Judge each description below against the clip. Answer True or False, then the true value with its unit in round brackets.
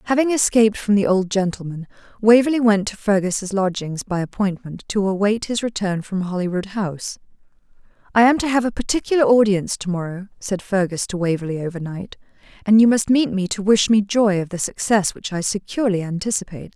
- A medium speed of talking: True (180 wpm)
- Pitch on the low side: False (200 Hz)